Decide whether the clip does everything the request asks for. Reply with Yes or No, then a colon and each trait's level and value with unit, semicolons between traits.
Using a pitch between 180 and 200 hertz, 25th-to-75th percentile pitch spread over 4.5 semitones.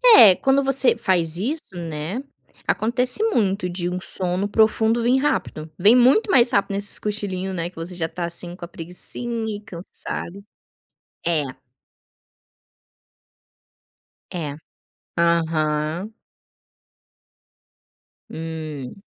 Yes: medium, 185 Hz; average, 5.2 semitones